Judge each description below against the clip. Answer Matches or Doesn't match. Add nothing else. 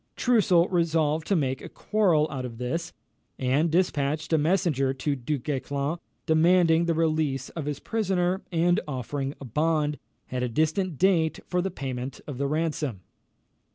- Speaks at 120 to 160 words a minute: Matches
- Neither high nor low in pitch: Matches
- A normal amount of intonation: Matches